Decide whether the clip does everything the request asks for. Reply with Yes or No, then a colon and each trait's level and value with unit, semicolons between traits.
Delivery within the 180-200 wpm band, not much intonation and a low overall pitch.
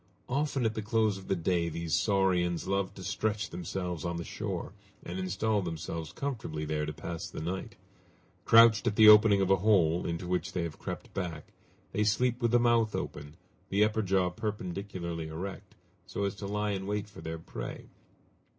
No: average, 185 wpm; average, 3.9 semitones; very low, 95 Hz